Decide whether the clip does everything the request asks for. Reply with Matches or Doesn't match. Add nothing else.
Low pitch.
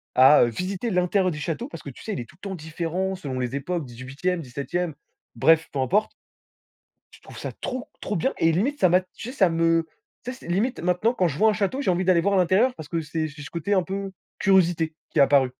Doesn't match